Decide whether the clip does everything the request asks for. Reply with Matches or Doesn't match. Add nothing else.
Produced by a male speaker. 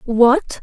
Doesn't match